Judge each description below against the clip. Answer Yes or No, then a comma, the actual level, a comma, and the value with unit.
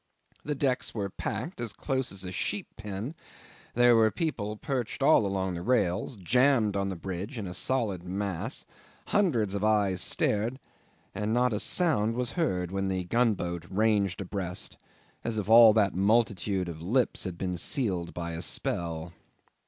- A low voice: Yes, low, 105 Hz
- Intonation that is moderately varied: Yes, average, 4.2 semitones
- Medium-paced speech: Yes, average, 165 wpm